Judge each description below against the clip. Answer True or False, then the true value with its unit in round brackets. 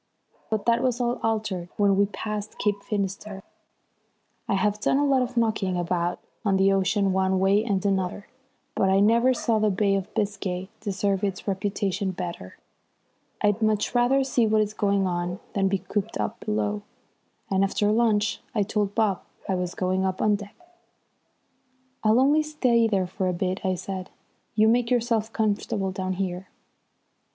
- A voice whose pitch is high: True (200 Hz)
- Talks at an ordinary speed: True (170 wpm)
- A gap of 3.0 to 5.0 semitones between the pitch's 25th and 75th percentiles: False (2.4 semitones)